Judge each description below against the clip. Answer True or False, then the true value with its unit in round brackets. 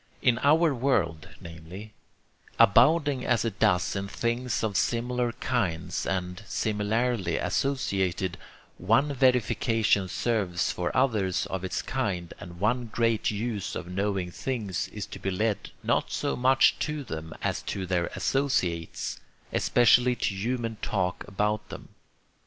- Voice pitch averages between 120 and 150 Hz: False (105 Hz)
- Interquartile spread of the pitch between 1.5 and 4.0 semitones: False (5.0 semitones)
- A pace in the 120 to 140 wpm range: True (135 wpm)